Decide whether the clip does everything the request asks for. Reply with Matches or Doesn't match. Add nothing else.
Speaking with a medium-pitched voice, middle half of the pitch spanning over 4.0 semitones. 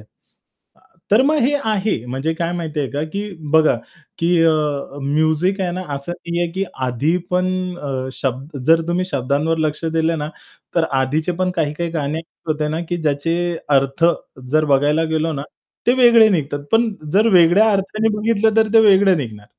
Matches